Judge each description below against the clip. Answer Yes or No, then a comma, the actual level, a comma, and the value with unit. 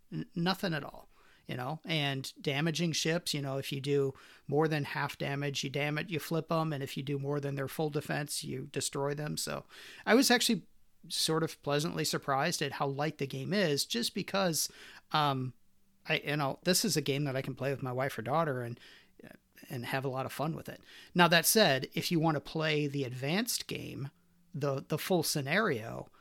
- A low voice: No, medium, 150 Hz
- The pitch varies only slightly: No, average, 3.3 semitones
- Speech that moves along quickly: Yes, fast, 215 wpm